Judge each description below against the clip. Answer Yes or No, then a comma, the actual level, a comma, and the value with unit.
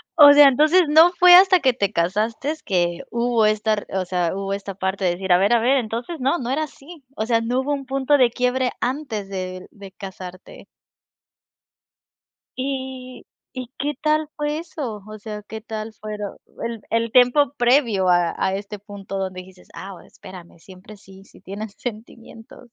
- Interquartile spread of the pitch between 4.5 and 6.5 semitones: Yes, average, 5.2 semitones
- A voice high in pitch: Yes, high, 225 Hz